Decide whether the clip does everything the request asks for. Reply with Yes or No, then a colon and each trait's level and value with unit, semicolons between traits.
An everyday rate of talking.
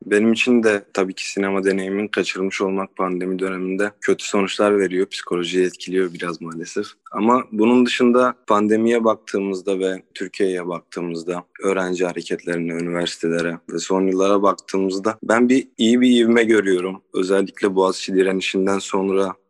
Yes: average, 130 wpm